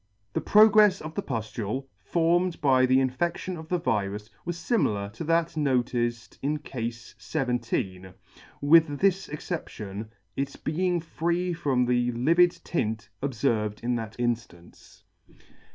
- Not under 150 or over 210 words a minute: No, slow, 135 wpm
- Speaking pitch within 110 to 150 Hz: Yes, low, 135 Hz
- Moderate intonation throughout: No, wide, 6.4 semitones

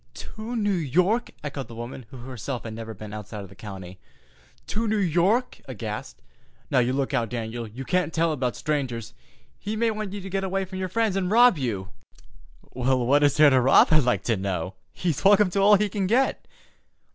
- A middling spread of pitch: No, wide, 8.7 semitones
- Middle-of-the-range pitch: Yes, medium, 145 Hz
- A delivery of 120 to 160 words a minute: No, average, 200 wpm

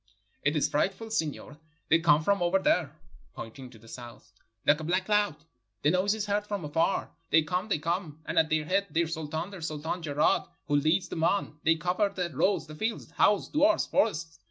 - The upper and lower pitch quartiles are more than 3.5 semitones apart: Yes, average, 4.4 semitones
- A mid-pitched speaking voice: Yes, medium, 165 Hz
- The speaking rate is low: No, fast, 205 wpm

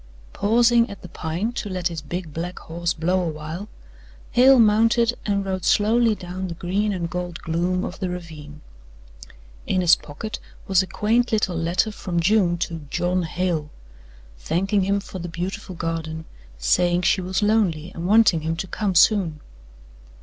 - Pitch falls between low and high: Yes, medium, 180 Hz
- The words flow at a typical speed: Yes, average, 170 wpm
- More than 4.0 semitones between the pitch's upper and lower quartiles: No, average, 3.5 semitones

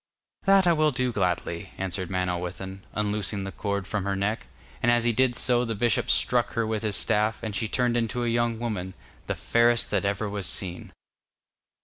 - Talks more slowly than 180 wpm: No, average, 190 wpm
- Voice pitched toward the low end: Yes, low, 105 Hz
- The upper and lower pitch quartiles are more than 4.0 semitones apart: No, average, 3.5 semitones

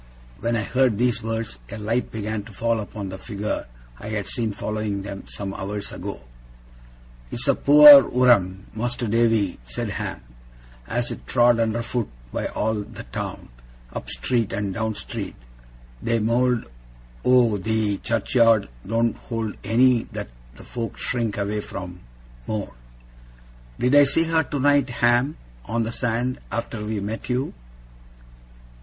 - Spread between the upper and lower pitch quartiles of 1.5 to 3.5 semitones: Yes, average, 2.7 semitones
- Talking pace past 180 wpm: No, average, 150 wpm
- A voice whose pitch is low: Yes, low, 115 Hz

